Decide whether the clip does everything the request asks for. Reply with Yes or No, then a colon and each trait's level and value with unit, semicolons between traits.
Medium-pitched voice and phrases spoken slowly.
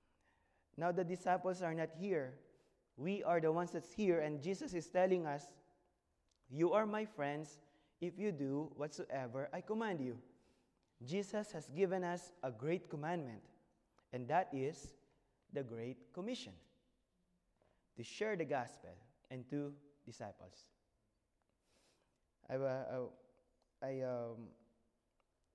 Yes: medium, 150 Hz; slow, 120 wpm